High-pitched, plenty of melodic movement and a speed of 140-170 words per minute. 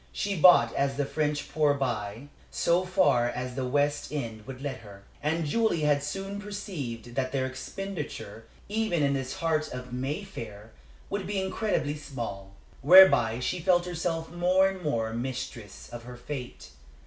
No: medium, 145 Hz; wide, 6.4 semitones; average, 160 wpm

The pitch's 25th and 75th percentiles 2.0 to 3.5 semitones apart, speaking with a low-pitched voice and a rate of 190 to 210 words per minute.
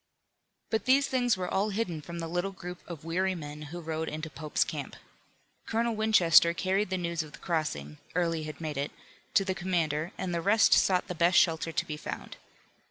No: average, 3.1 semitones; medium, 170 Hz; average, 200 wpm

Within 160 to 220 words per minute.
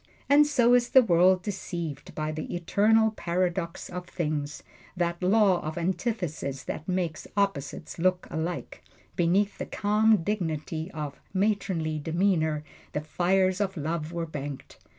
No: slow, 135 wpm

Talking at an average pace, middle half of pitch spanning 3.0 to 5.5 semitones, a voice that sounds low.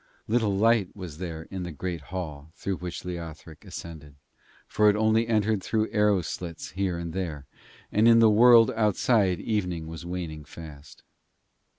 Yes: average, 160 wpm; average, 4.5 semitones; very low, 90 Hz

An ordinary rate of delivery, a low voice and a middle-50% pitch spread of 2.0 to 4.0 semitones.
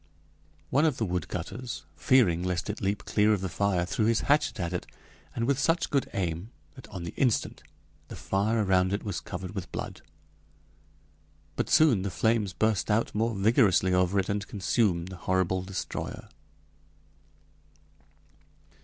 Yes: average, 155 wpm; low, 100 Hz; average, 3.6 semitones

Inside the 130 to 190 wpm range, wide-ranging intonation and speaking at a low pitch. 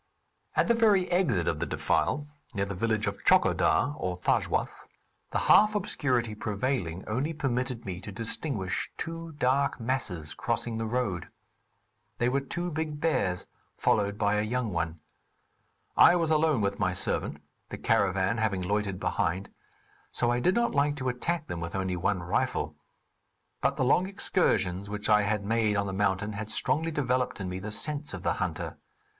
Yes: average, 170 wpm; wide, 6.7 semitones; low, 110 Hz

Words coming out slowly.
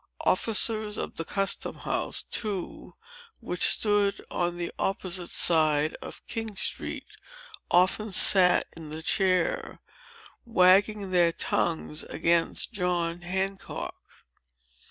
Yes: slow, 105 wpm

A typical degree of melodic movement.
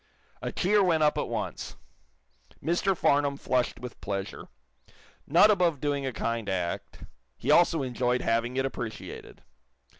No: wide, 5.7 semitones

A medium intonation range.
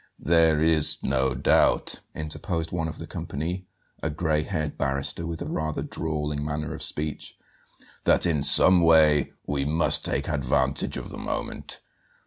No: narrow, 2.0 semitones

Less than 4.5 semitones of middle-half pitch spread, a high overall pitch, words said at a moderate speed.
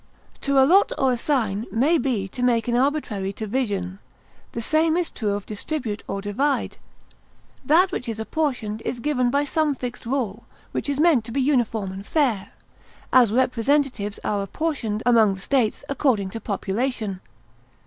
No: average, 5.0 semitones; high, 245 Hz; average, 160 wpm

